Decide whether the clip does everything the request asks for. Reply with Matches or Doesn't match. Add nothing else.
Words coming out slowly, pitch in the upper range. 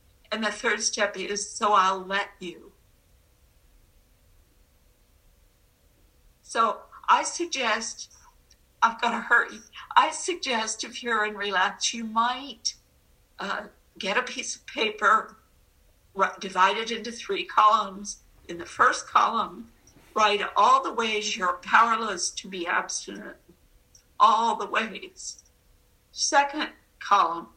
Matches